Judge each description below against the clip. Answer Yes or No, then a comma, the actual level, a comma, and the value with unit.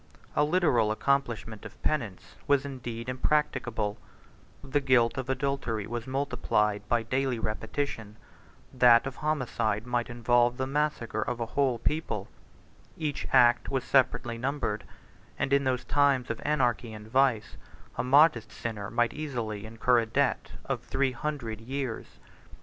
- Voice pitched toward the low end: Yes, low, 125 Hz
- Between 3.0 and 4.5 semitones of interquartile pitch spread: Yes, average, 3.3 semitones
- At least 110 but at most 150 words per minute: Yes, average, 140 wpm